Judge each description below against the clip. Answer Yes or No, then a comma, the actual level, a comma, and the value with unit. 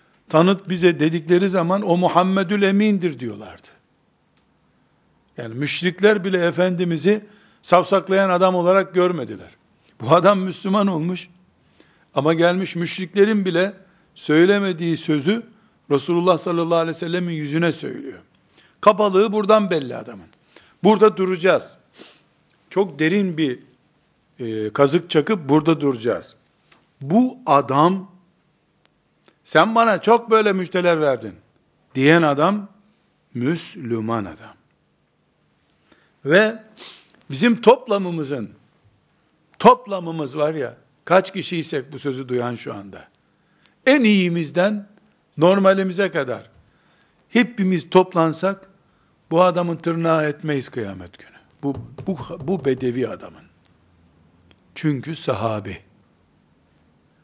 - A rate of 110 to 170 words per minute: No, slow, 95 wpm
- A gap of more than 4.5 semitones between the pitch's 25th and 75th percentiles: Yes, average, 5.1 semitones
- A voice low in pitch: No, medium, 175 Hz